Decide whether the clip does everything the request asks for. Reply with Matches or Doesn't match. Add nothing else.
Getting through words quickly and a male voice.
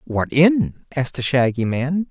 Doesn't match